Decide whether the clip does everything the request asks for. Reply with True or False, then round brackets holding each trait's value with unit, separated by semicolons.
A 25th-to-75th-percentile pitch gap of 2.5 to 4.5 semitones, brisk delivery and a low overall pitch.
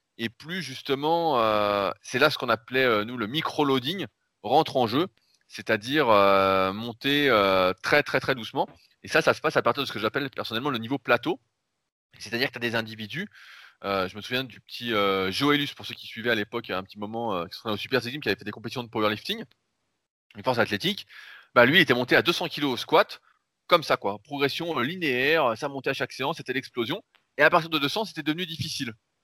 False (5.2 semitones; 225 wpm; 125 Hz)